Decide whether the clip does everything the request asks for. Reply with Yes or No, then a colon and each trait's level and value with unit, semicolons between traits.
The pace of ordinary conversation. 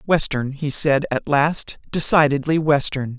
No: slow, 130 wpm